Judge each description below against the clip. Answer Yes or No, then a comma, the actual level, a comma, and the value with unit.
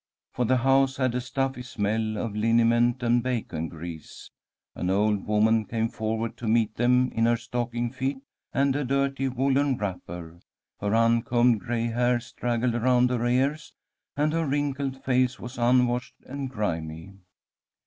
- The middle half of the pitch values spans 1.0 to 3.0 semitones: Yes, narrow, 2.6 semitones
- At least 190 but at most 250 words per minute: No, average, 150 wpm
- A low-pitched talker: Yes, low, 120 Hz